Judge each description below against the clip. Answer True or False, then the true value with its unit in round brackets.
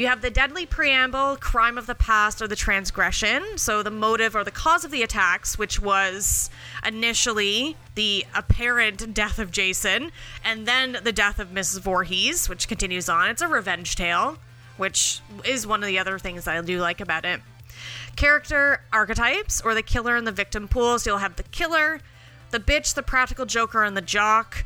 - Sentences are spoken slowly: False (190 wpm)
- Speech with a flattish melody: False (4.0 semitones)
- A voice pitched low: False (220 Hz)